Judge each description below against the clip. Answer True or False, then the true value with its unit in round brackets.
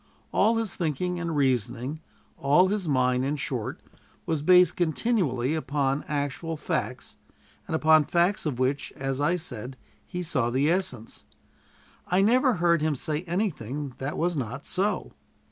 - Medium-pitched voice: True (150 Hz)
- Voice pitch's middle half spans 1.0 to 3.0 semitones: False (4.8 semitones)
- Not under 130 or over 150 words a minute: True (145 wpm)